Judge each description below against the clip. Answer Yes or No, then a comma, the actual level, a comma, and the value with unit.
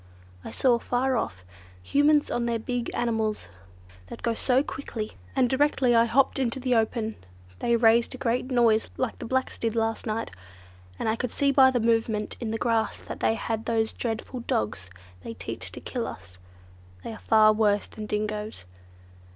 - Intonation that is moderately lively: No, narrow, 2.3 semitones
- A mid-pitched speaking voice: No, high, 230 Hz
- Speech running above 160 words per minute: Yes, average, 180 wpm